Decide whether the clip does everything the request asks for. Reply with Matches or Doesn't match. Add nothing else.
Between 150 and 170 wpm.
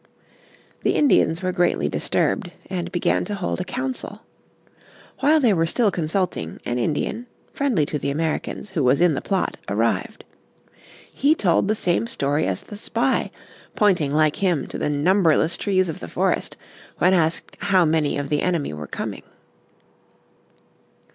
Matches